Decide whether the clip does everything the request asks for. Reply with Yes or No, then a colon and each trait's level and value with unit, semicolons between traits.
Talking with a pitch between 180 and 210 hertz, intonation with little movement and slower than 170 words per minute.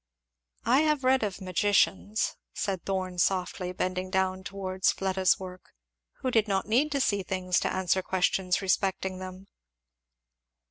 Yes: high, 190 Hz; narrow, 1.6 semitones; average, 140 wpm